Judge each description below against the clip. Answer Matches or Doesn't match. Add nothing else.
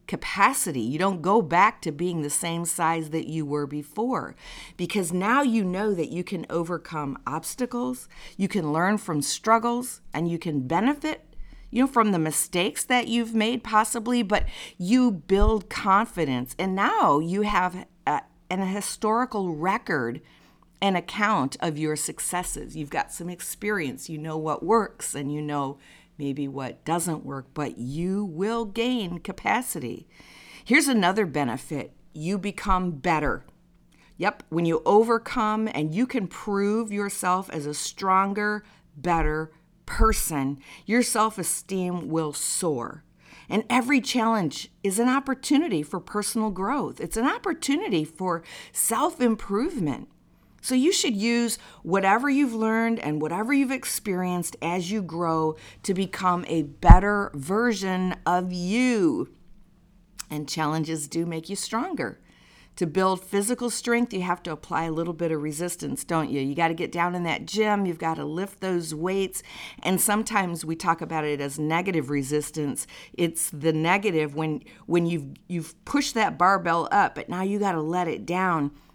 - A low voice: Doesn't match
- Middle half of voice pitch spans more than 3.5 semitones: Matches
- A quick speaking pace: Doesn't match